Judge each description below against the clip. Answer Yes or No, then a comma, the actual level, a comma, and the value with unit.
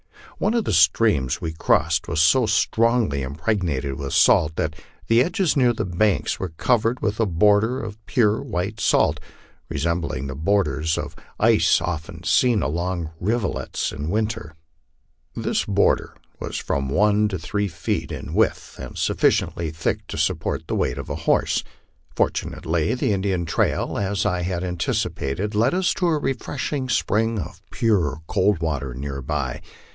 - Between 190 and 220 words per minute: No, average, 160 wpm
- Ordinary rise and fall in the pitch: No, wide, 5.8 semitones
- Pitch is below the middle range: Yes, very low, 95 Hz